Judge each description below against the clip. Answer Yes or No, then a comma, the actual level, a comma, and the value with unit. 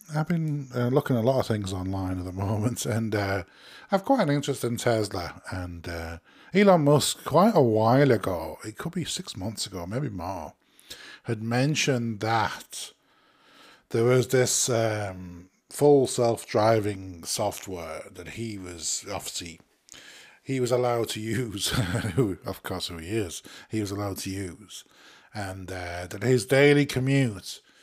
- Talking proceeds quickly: No, average, 155 wpm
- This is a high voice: No, low, 115 Hz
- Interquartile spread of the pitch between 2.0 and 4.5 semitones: No, wide, 5.4 semitones